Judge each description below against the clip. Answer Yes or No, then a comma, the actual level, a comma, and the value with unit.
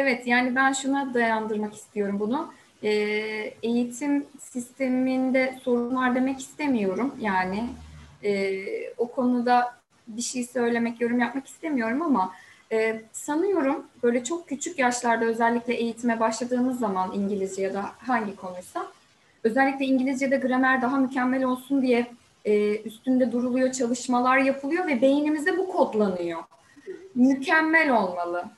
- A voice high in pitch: Yes, high, 245 Hz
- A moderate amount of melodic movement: Yes, average, 3.4 semitones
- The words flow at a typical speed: Yes, average, 120 wpm